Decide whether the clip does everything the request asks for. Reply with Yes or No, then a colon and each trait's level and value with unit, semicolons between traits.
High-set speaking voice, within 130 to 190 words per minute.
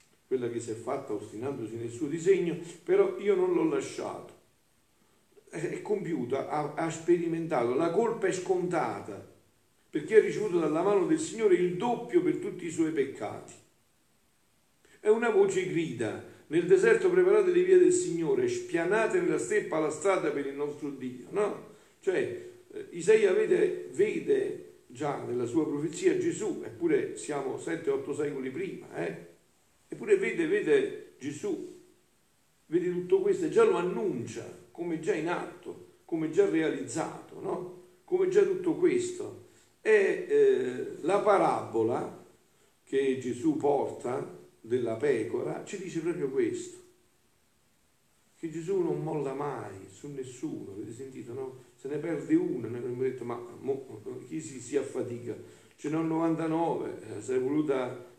Yes: very high, 365 Hz; average, 140 wpm